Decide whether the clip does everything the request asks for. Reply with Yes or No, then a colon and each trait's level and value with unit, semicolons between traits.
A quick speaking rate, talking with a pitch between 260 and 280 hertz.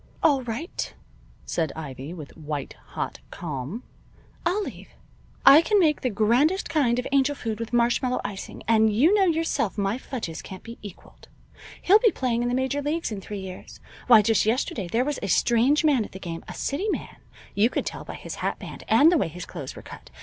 No: fast, 210 wpm; high, 235 Hz